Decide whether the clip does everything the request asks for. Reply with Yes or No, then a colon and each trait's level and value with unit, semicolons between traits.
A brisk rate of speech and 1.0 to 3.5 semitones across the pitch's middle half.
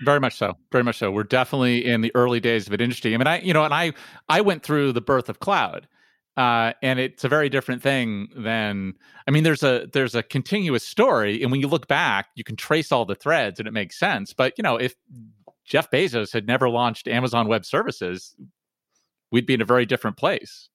Yes: fast, 230 wpm; average, 3.1 semitones